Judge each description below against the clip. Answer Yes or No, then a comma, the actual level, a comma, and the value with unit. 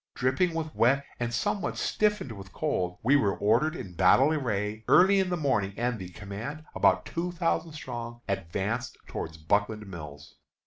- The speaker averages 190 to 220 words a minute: No, average, 165 wpm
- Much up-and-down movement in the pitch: Yes, wide, 7.6 semitones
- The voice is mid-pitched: No, low, 120 Hz